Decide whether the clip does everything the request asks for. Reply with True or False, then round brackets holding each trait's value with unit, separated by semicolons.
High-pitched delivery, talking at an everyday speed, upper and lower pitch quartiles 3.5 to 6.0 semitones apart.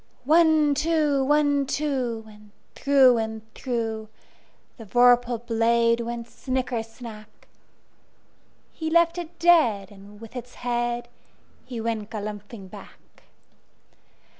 False (240 Hz; 95 wpm; 4.0 semitones)